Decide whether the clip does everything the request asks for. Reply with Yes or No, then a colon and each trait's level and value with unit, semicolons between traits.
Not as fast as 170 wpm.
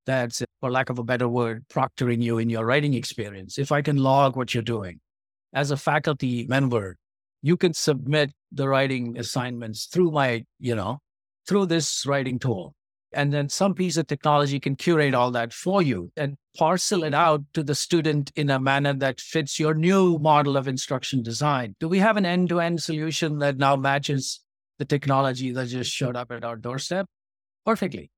No: average, 190 wpm